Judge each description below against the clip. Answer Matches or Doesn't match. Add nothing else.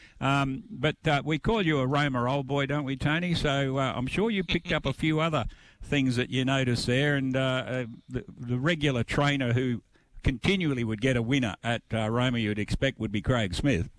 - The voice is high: Doesn't match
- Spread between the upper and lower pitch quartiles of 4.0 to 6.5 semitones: Doesn't match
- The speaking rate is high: Matches